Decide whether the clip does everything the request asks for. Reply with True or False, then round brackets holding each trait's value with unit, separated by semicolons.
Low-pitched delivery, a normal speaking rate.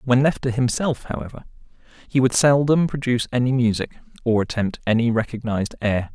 True (120 Hz; 155 wpm)